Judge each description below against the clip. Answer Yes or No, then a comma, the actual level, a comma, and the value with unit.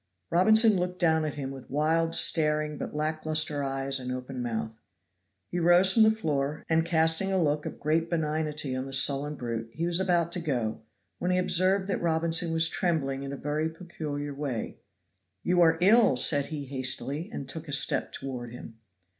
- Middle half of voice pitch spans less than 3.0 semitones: No, average, 3.8 semitones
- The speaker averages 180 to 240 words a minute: Yes, average, 190 wpm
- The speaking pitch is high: No, medium, 155 Hz